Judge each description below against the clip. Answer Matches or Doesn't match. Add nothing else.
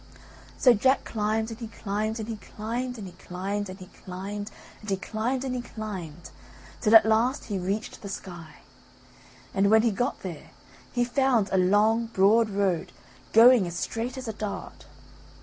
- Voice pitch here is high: Matches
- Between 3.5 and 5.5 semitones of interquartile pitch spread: Doesn't match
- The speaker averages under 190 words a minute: Matches